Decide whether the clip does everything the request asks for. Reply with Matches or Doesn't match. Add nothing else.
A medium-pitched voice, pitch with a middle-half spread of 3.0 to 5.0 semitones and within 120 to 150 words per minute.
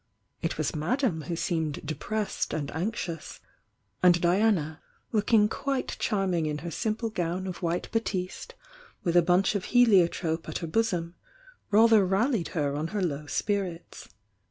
Matches